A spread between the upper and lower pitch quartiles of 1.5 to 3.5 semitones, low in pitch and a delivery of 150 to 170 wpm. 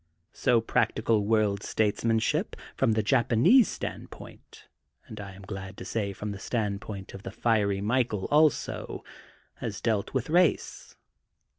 No: average, 2.7 semitones; low, 110 Hz; slow, 135 wpm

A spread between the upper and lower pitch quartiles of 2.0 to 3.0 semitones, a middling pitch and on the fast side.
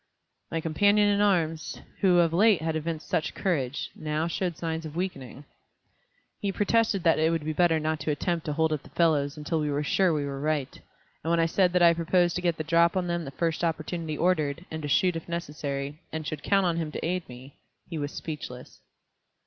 Yes: narrow, 2.5 semitones; medium, 165 Hz; fast, 220 wpm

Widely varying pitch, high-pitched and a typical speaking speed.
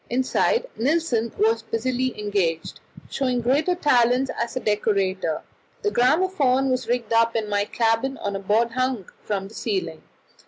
No: average, 3.7 semitones; high, 230 Hz; average, 150 wpm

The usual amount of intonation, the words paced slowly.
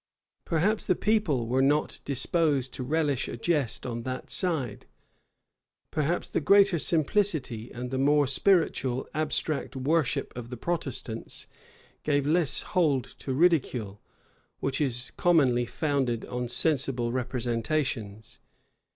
Yes: average, 4.4 semitones; slow, 120 wpm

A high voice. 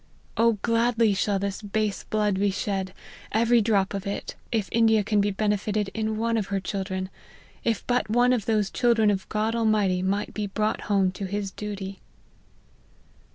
Yes: high, 210 Hz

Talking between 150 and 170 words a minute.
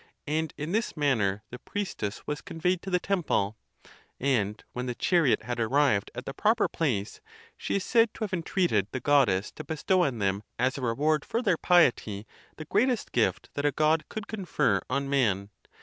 No: average, 190 wpm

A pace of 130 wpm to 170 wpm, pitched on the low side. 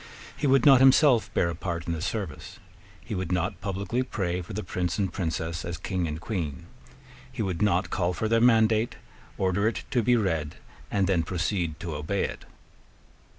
No: average, 190 wpm; very low, 95 Hz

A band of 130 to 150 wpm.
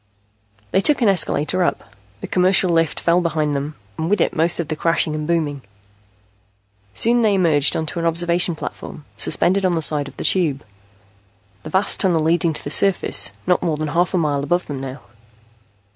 No: average, 190 wpm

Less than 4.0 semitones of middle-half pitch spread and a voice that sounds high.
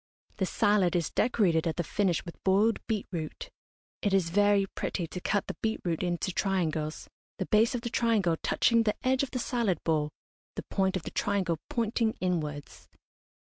No: average, 4.4 semitones; high, 195 Hz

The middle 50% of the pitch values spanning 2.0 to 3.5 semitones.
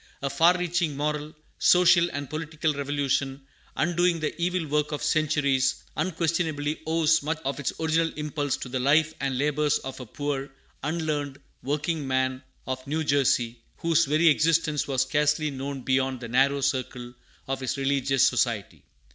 Yes: average, 2.8 semitones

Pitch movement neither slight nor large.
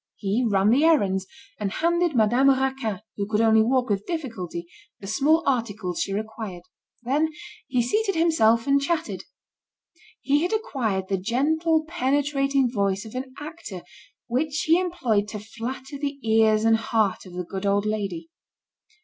No: wide, 5.8 semitones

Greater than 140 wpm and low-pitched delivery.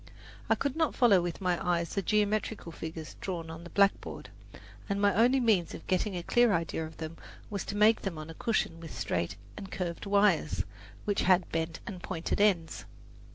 No: average, 195 wpm; medium, 185 Hz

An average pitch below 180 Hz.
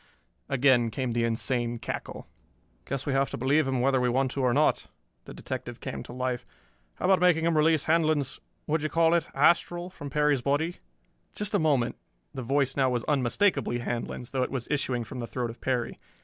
Yes: low, 135 Hz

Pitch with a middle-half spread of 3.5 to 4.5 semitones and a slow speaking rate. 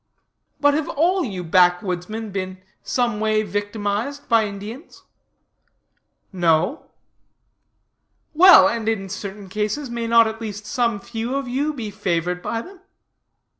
Yes: average, 3.8 semitones; slow, 130 wpm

